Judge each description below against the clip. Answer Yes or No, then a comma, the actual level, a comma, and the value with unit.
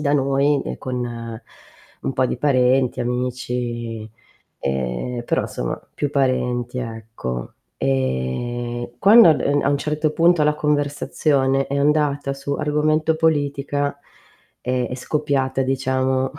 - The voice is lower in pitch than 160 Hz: Yes, low, 135 Hz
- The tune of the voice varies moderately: Yes, average, 3.1 semitones